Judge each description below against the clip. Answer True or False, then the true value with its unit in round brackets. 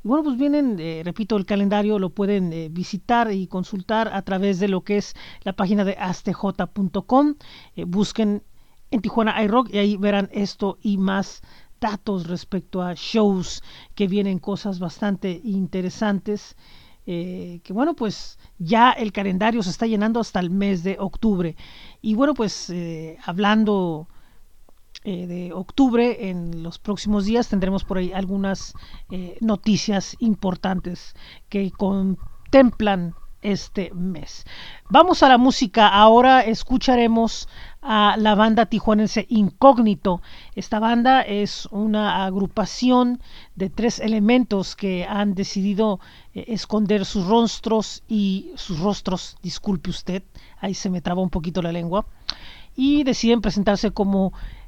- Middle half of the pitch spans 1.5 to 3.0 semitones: True (2.7 semitones)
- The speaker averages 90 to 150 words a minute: True (135 wpm)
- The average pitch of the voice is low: False (205 Hz)